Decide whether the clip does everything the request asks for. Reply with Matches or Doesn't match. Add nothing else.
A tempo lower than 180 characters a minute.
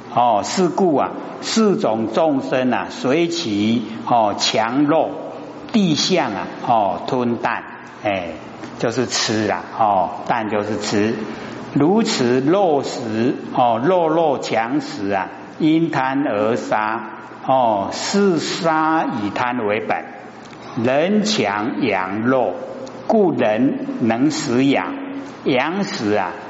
Matches